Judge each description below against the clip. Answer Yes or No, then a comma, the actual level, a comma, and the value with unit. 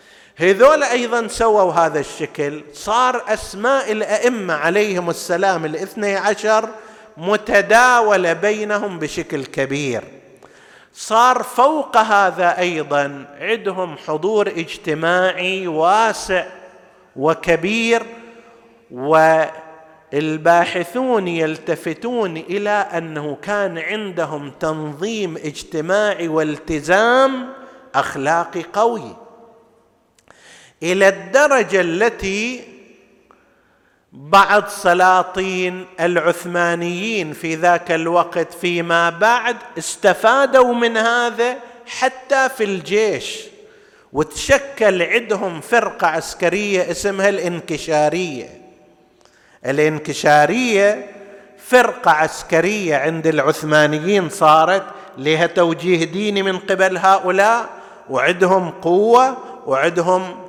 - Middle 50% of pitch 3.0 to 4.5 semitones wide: No, average, 5.1 semitones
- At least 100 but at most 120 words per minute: No, average, 75 wpm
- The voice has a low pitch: No, high, 190 Hz